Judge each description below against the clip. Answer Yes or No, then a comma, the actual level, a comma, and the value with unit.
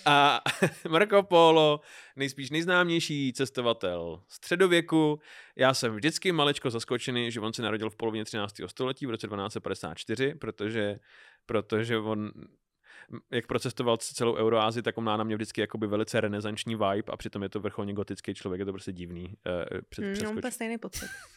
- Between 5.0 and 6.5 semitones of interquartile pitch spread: Yes, wide, 5.5 semitones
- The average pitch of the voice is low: Yes, low, 115 Hz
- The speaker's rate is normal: Yes, average, 150 wpm